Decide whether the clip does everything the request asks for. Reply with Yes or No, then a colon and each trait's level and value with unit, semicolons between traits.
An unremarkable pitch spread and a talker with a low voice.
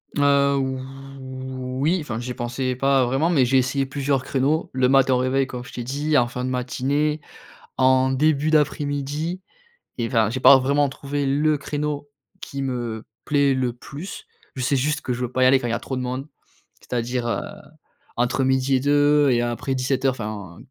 No: narrow, 2.2 semitones; low, 130 Hz